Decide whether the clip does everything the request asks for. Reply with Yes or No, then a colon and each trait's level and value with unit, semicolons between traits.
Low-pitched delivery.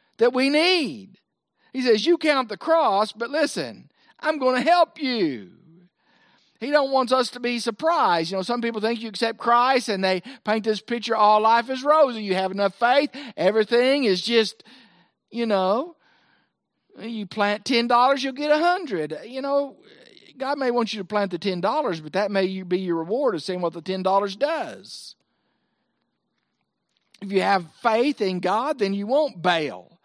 No: high, 230 Hz